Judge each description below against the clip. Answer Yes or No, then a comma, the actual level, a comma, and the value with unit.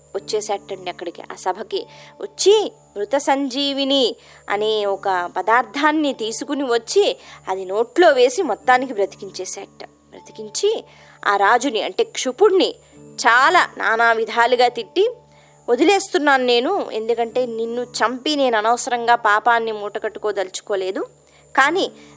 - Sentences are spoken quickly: No, average, 95 wpm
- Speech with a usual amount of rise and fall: No, wide, 5.9 semitones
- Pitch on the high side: Yes, high, 235 Hz